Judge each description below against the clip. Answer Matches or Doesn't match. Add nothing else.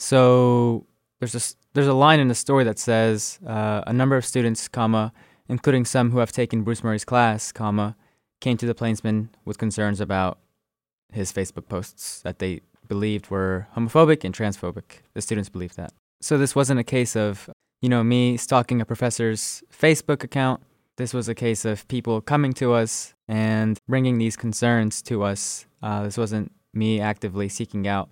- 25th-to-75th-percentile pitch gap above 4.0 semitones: Doesn't match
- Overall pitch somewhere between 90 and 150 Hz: Matches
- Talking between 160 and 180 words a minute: Matches